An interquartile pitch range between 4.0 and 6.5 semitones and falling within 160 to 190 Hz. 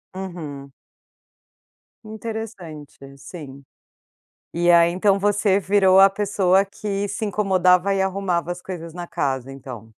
No: average, 3.1 semitones; medium, 185 Hz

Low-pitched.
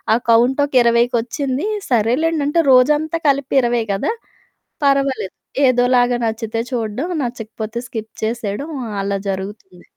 No: high, 240 Hz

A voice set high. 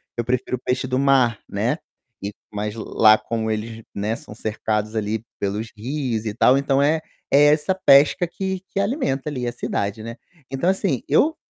No: low, 125 Hz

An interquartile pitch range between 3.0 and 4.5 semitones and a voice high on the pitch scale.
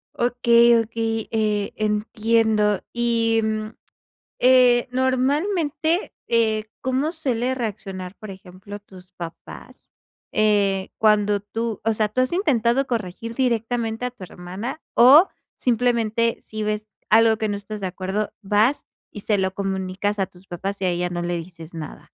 Yes: average, 3.3 semitones; high, 215 Hz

